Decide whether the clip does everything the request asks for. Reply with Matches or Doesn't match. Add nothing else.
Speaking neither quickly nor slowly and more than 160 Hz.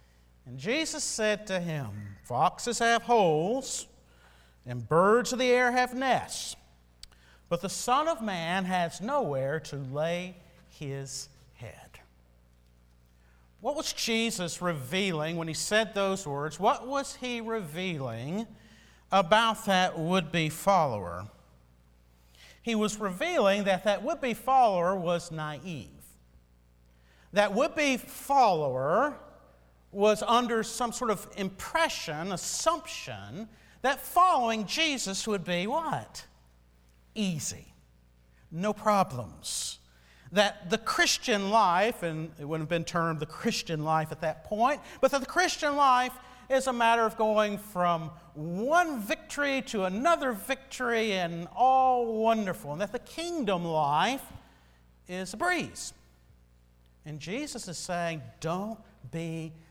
Doesn't match